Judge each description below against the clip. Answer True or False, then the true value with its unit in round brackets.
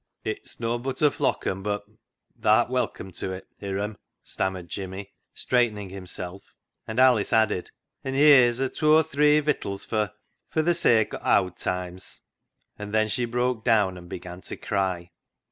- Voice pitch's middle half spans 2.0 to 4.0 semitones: False (4.8 semitones)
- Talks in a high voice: False (110 Hz)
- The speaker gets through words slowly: False (165 wpm)